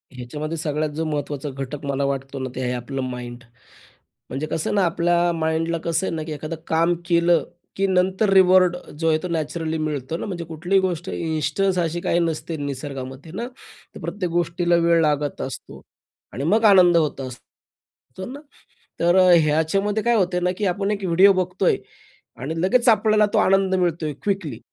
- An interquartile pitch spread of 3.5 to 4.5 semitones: Yes, average, 3.8 semitones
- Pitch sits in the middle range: Yes, medium, 165 Hz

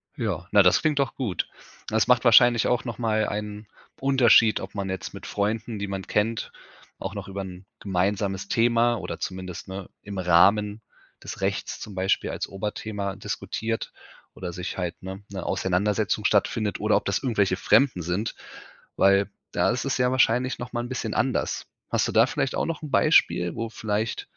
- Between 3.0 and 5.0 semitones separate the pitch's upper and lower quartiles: Yes, average, 3.3 semitones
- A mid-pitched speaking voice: No, low, 105 Hz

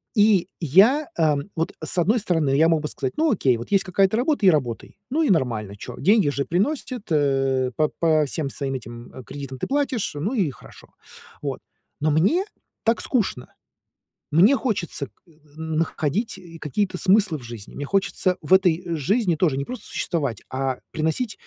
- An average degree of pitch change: No, wide, 6.7 semitones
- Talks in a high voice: No, medium, 165 Hz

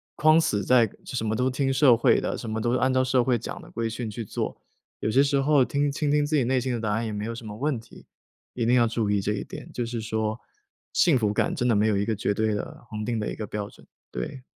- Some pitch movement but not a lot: Yes, average, 3.2 semitones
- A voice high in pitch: No, low, 115 Hz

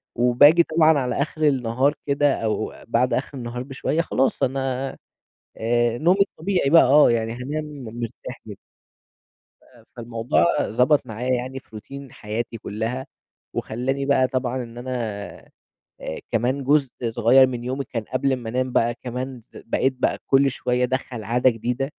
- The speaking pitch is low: Yes, low, 130 Hz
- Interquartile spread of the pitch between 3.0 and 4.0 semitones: No, narrow, 2.5 semitones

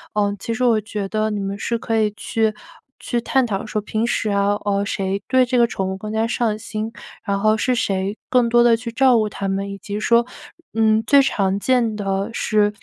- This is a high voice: Yes, high, 215 Hz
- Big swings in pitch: No, narrow, 2.6 semitones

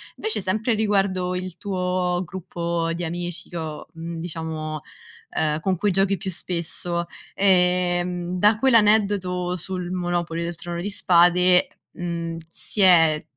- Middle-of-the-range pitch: Yes, medium, 180 Hz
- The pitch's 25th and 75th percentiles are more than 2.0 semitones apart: No, narrow, 1.7 semitones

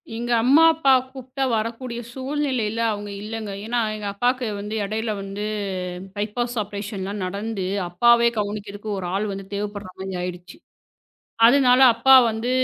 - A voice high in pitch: Yes, high, 215 Hz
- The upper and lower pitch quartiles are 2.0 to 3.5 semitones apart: Yes, average, 3.1 semitones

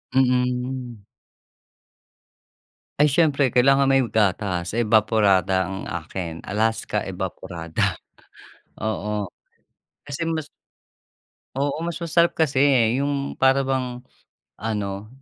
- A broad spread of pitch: Yes, wide, 5.7 semitones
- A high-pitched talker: No, low, 120 Hz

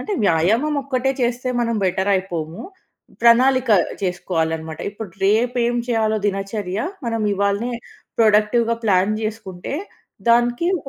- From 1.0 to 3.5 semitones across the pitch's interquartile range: No, average, 4.1 semitones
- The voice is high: Yes, high, 215 Hz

